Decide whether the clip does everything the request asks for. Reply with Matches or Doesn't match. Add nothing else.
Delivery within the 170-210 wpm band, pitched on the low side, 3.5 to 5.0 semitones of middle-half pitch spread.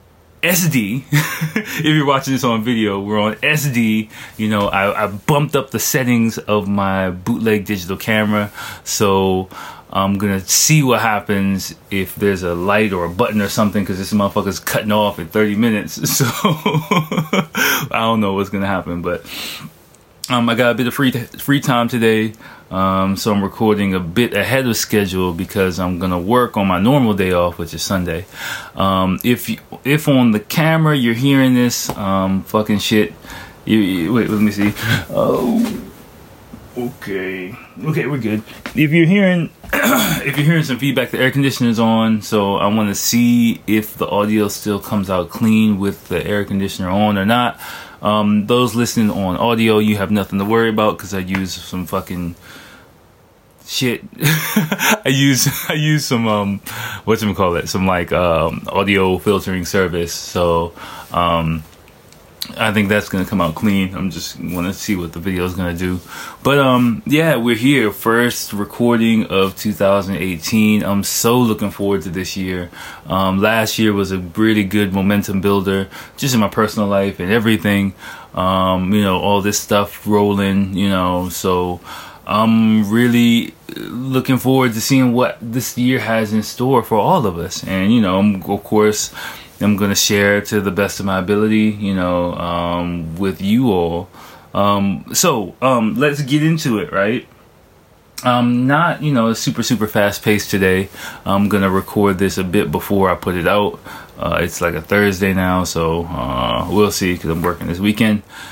Matches